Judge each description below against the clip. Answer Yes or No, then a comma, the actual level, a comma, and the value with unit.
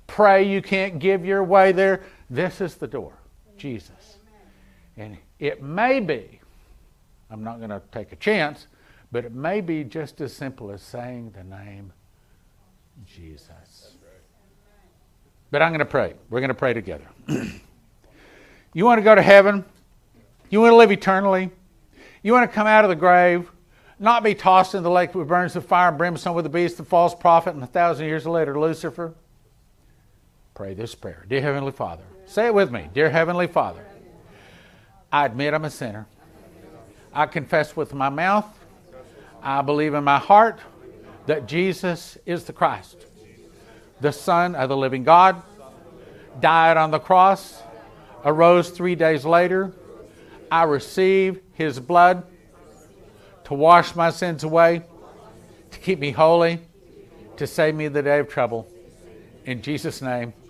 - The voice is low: No, medium, 160 Hz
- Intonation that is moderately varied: No, wide, 6.3 semitones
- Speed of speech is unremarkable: Yes, average, 160 wpm